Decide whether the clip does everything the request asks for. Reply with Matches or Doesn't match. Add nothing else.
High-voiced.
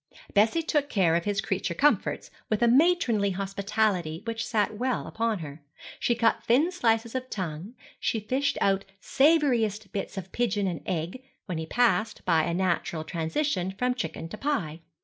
Matches